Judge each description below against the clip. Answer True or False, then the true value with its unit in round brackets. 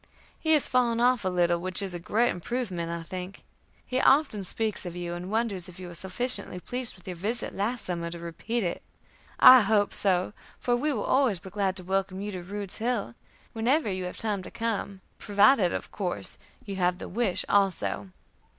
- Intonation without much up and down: False (4.4 semitones)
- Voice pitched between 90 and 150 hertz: False (195 Hz)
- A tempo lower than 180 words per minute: False (200 wpm)